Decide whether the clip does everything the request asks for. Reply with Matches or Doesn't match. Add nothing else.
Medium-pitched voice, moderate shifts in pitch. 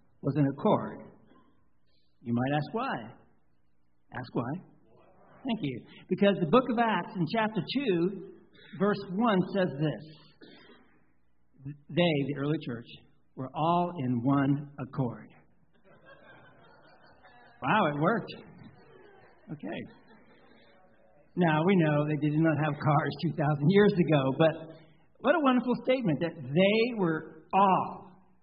Matches